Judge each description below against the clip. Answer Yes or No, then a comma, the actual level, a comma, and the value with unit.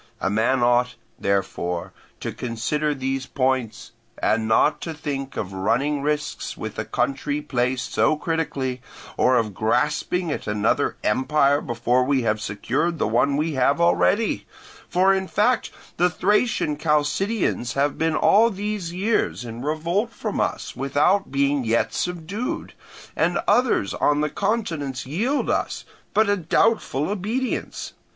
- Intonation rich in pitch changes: Yes, wide, 6.0 semitones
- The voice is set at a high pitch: No, medium, 145 Hz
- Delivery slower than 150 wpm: Yes, average, 140 wpm